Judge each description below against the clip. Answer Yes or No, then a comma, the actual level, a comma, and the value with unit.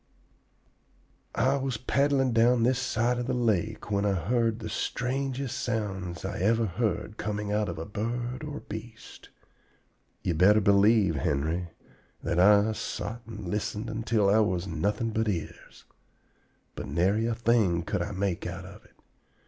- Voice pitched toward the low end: Yes, low, 105 Hz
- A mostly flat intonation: No, average, 3.5 semitones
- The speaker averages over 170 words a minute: No, average, 155 wpm